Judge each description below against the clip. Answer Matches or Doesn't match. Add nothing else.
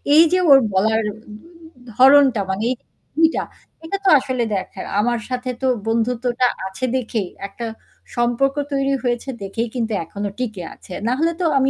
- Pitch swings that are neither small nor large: Matches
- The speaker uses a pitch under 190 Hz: Doesn't match